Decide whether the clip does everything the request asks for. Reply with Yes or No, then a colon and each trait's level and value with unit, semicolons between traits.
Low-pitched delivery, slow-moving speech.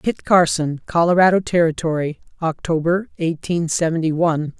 No: medium, 165 Hz; slow, 105 wpm